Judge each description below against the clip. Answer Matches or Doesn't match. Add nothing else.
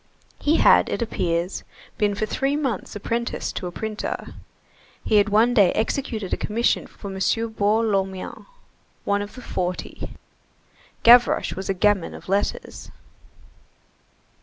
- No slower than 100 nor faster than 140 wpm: Matches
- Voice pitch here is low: Doesn't match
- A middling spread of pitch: Matches